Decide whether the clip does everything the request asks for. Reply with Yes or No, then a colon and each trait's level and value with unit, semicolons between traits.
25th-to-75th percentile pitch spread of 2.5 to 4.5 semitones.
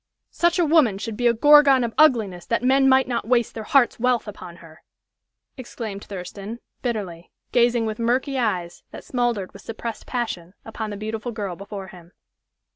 Yes: average, 4.0 semitones